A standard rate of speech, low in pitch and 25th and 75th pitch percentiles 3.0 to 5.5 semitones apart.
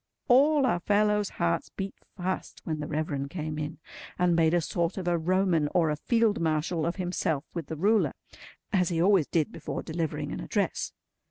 No: average, 185 wpm; medium, 170 Hz; average, 3.4 semitones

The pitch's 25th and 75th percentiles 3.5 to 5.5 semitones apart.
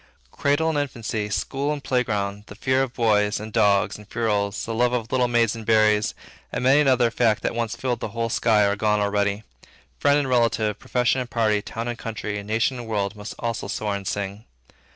No: average, 2.9 semitones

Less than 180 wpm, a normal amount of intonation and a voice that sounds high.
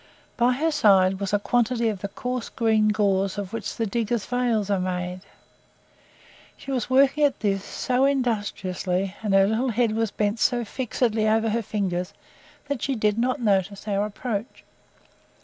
Yes: average, 165 wpm; average, 3.6 semitones; high, 215 Hz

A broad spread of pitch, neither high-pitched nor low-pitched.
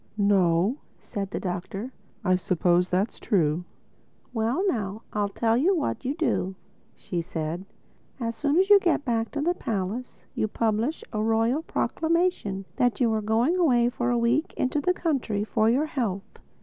No: wide, 6.1 semitones; high, 225 Hz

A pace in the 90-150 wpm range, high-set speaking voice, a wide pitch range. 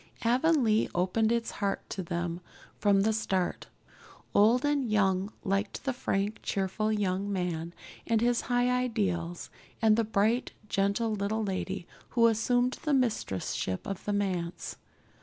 No: average, 140 wpm; high, 210 Hz; average, 3.4 semitones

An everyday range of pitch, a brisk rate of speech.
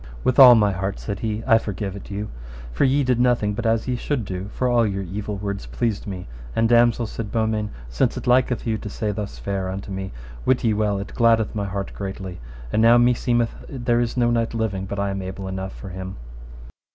Yes: average, 3.3 semitones; fast, 225 wpm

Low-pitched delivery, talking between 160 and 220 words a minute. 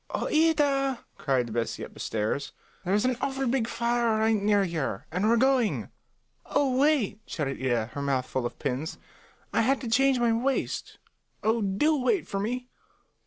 No: high, 225 Hz; average, 170 wpm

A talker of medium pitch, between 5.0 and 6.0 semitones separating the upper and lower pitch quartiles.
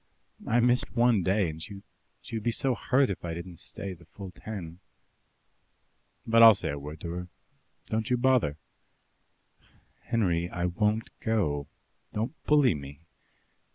No: low, 100 Hz; average, 5.3 semitones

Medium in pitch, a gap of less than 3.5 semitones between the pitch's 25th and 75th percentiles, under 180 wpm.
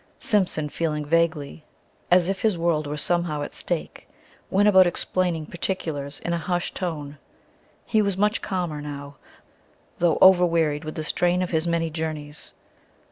Yes: medium, 165 Hz; average, 3.0 semitones; average, 150 wpm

